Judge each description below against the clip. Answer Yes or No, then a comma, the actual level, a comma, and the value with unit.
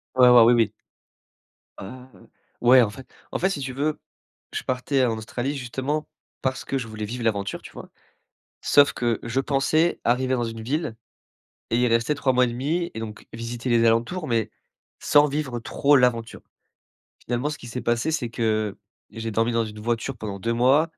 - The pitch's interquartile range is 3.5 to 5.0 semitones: No, average, 2.9 semitones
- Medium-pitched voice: No, low, 120 Hz